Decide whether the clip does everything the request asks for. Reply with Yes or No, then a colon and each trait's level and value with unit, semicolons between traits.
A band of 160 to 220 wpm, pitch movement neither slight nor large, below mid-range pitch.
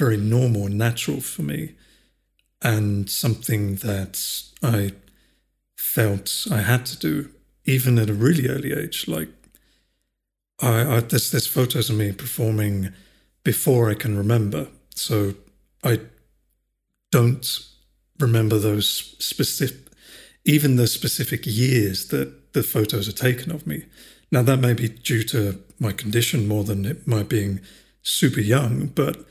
No: slow, 135 wpm; average, 3.6 semitones; low, 115 Hz